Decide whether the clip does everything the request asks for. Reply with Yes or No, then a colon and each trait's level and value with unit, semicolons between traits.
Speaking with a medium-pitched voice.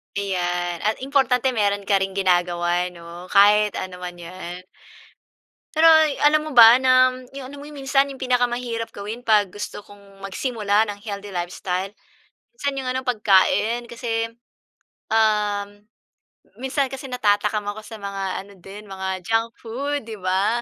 No: high, 210 Hz